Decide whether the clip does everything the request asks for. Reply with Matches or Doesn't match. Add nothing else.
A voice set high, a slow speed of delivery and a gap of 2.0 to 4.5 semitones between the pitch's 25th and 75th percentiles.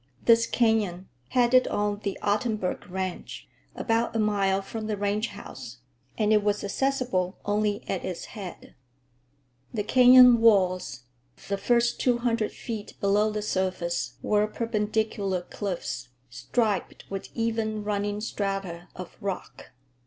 Matches